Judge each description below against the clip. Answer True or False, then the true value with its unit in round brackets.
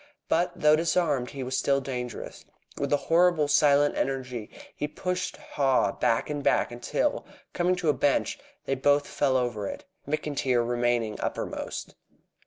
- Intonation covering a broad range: False (3.3 semitones)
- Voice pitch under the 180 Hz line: True (140 Hz)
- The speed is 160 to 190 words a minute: False (150 wpm)